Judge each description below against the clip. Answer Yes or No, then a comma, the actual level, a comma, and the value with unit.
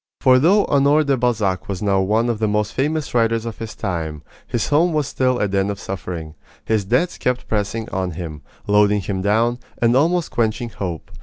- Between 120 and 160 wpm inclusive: No, average, 200 wpm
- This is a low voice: Yes, low, 110 Hz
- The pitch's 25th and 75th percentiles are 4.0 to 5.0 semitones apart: Yes, average, 4.7 semitones